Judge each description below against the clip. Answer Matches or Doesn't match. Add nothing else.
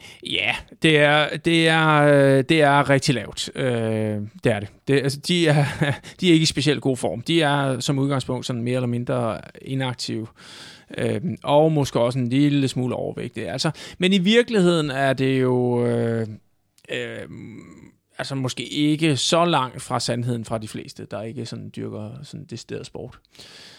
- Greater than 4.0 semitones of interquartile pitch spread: Doesn't match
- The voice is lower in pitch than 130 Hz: Doesn't match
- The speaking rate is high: Doesn't match